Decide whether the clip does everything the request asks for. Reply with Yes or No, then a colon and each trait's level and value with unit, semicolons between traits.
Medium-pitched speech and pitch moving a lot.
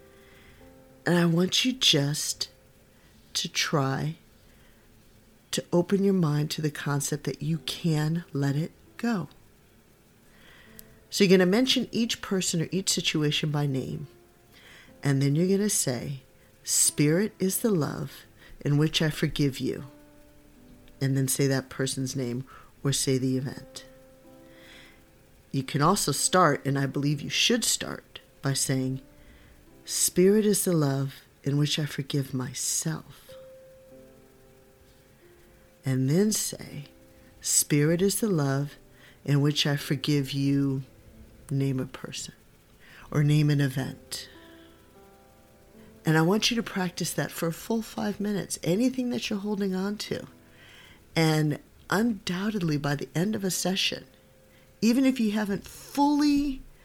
Yes: medium, 145 Hz; wide, 5.8 semitones